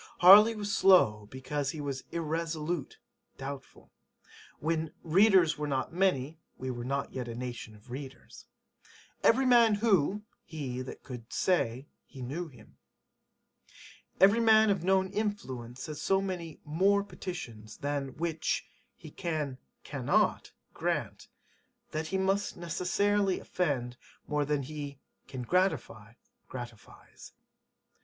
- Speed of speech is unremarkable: No, slow, 125 wpm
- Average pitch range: No, wide, 6.5 semitones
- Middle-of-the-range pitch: Yes, medium, 155 Hz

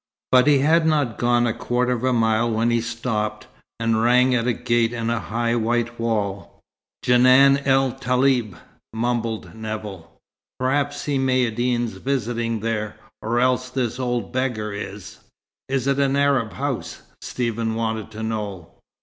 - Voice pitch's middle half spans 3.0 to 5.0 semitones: No, narrow, 2.4 semitones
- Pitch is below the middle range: Yes, low, 120 Hz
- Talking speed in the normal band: Yes, average, 150 wpm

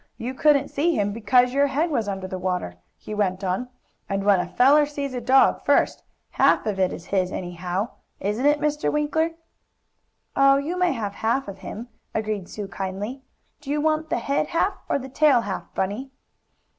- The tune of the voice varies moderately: No, wide, 6.5 semitones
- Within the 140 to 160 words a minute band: No, average, 190 wpm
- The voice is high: Yes, high, 245 Hz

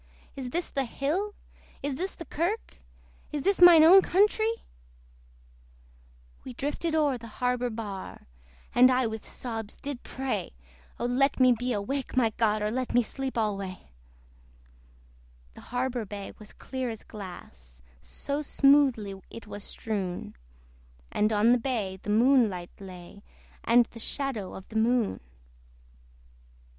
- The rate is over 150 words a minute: No, average, 140 wpm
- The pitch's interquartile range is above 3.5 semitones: Yes, average, 4.6 semitones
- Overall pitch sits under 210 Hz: No, high, 245 Hz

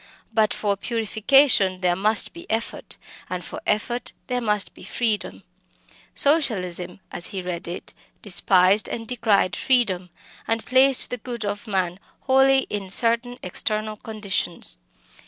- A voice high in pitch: Yes, high, 215 Hz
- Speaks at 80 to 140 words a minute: Yes, slow, 135 wpm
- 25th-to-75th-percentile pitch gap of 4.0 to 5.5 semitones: Yes, average, 4.4 semitones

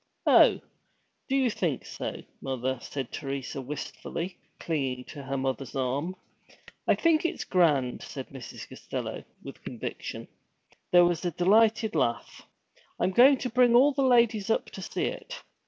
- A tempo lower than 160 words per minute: Yes, average, 150 wpm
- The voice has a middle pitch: Yes, medium, 175 Hz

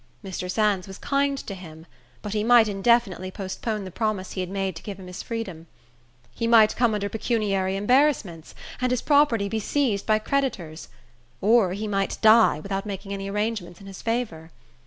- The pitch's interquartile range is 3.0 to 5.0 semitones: Yes, average, 3.3 semitones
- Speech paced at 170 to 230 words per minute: Yes, average, 180 wpm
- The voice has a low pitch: No, high, 205 Hz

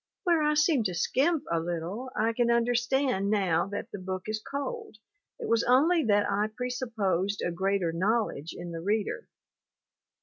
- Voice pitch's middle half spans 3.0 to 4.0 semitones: No, average, 5.3 semitones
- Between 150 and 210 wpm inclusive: Yes, average, 165 wpm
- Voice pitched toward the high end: Yes, high, 215 Hz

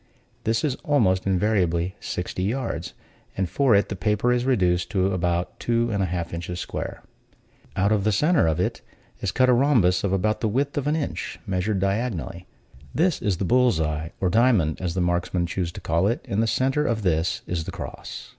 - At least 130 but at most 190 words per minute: No, average, 200 wpm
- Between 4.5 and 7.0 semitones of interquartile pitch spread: Yes, average, 5.1 semitones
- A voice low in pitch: Yes, low, 100 Hz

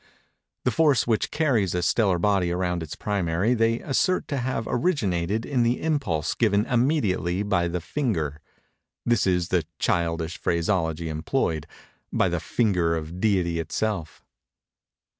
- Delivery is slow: Yes, slow, 130 wpm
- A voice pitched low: Yes, very low, 95 Hz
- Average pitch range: No, wide, 5.7 semitones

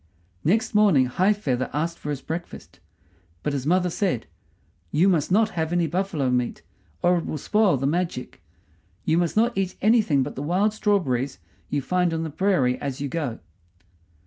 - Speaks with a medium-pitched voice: Yes, medium, 165 Hz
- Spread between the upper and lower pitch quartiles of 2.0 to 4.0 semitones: No, average, 5.3 semitones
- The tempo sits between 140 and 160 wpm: No, average, 175 wpm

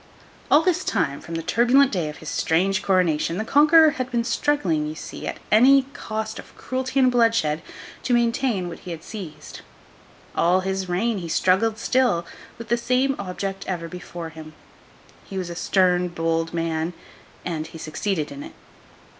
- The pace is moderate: Yes, average, 170 wpm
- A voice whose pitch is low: No, high, 190 Hz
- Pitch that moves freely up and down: Yes, wide, 6.2 semitones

